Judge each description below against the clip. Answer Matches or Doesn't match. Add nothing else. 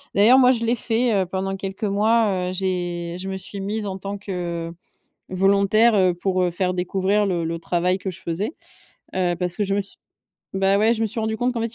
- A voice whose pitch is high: Matches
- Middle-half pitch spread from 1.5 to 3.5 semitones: Matches